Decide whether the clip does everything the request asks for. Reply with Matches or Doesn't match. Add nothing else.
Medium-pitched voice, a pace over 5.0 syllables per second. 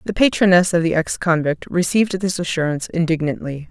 Matches